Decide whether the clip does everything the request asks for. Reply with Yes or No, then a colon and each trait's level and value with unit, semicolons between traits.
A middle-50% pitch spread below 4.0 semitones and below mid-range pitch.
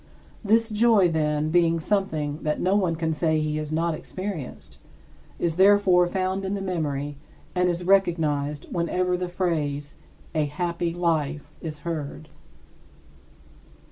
No: average, 3.3 semitones; medium, 170 Hz